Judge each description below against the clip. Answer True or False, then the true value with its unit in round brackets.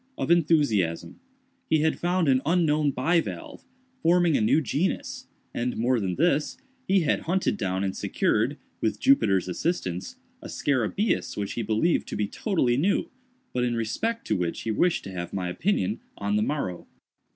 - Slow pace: False (165 wpm)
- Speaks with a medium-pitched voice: False (130 Hz)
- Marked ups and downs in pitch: True (8.5 semitones)